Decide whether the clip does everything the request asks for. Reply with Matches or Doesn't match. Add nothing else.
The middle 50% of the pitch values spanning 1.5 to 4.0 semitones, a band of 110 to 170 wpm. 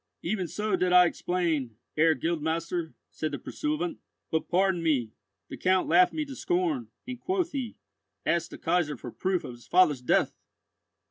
Matches